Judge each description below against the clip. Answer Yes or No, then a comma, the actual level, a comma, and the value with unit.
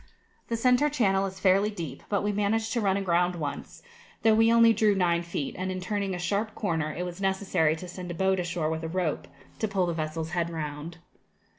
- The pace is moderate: No, fast, 220 wpm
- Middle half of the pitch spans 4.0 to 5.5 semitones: No, average, 3.4 semitones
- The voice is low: No, medium, 185 Hz